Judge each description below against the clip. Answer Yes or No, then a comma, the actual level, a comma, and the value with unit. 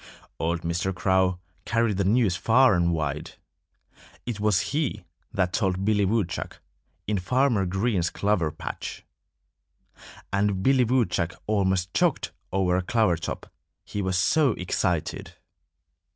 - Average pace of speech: No, slow, 125 wpm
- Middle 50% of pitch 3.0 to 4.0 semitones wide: Yes, average, 3.7 semitones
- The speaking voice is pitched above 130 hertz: No, very low, 95 Hz